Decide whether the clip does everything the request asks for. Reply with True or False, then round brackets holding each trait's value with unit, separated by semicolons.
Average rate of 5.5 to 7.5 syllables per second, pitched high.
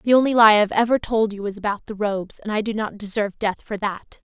True (6.3 syllables/s; 210 Hz)